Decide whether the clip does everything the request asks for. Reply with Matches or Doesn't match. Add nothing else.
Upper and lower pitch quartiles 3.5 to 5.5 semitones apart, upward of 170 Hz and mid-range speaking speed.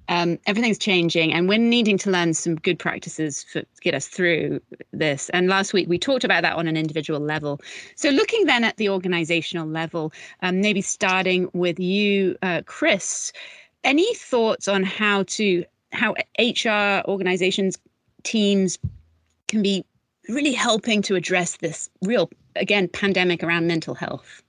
Matches